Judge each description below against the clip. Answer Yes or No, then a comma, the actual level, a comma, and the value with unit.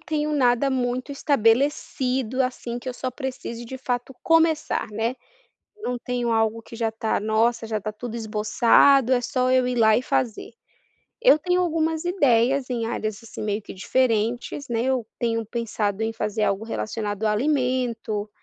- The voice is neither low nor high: No, high, 240 Hz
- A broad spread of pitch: No, average, 2.8 semitones